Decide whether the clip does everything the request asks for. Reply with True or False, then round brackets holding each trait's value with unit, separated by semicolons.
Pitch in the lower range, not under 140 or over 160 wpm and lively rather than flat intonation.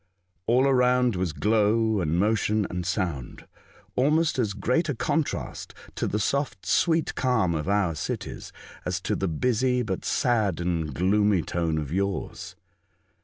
True (105 Hz; 145 wpm; 5.8 semitones)